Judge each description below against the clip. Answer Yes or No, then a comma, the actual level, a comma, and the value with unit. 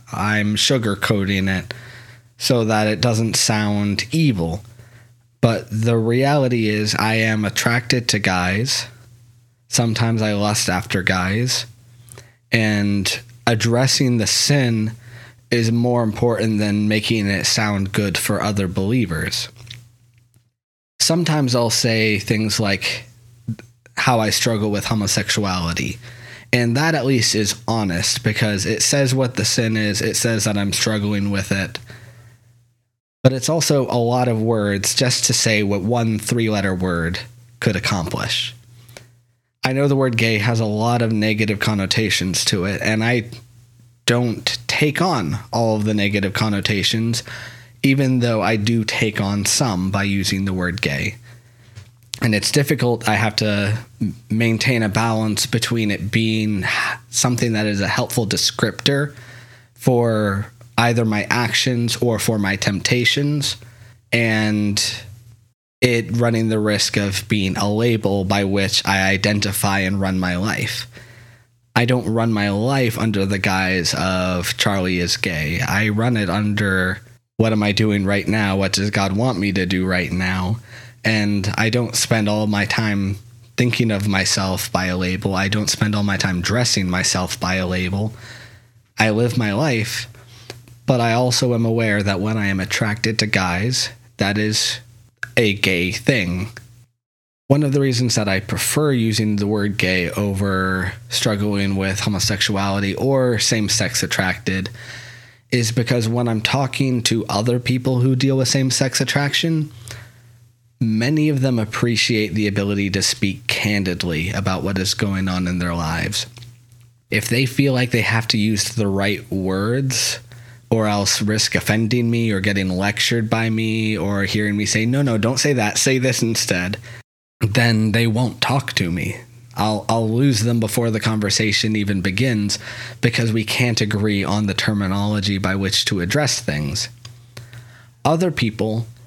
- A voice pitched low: Yes, low, 115 Hz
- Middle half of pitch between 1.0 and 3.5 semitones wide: Yes, average, 2.8 semitones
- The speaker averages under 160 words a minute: Yes, average, 150 wpm